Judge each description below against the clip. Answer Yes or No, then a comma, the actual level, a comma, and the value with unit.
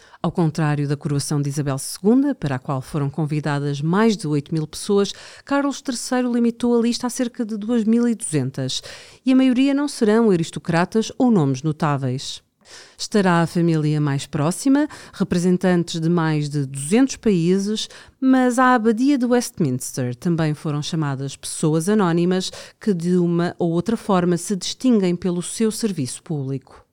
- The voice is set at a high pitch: No, medium, 175 Hz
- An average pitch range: No, wide, 7.3 semitones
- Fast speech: No, average, 150 wpm